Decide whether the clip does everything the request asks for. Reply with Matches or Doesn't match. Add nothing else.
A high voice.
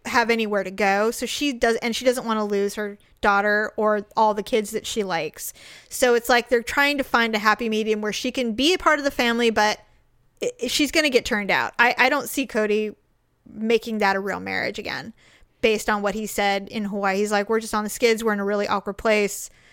Matches